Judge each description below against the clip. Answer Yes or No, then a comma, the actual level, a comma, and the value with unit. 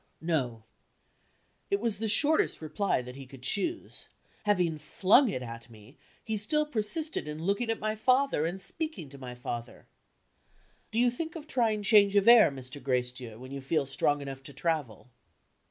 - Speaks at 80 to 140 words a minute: No, average, 170 wpm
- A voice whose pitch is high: No, medium, 170 Hz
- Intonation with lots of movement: Yes, wide, 9.0 semitones